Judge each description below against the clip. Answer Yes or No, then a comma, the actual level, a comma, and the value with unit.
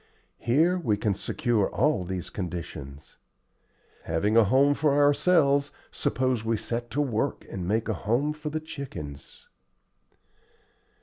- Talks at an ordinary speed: No, slow, 130 wpm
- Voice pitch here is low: Yes, low, 120 Hz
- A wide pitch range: Yes, wide, 6.6 semitones